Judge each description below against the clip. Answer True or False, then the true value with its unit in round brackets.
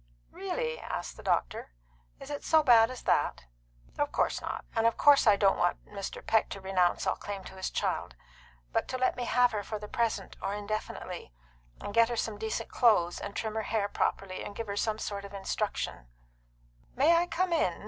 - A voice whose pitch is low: False (210 Hz)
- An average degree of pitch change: True (3.2 semitones)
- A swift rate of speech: True (210 wpm)